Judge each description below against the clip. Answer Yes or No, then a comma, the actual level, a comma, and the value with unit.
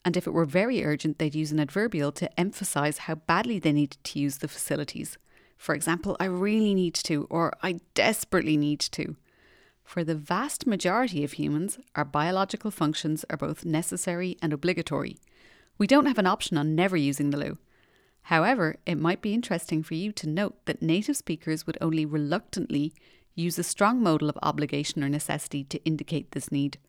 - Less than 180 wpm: No, average, 185 wpm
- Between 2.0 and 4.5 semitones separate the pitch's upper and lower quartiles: Yes, average, 3.5 semitones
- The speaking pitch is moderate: Yes, medium, 165 Hz